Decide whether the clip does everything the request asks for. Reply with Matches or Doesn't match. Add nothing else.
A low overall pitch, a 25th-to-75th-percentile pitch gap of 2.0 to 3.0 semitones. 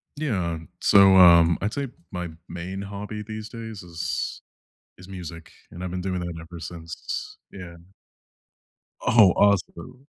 Doesn't match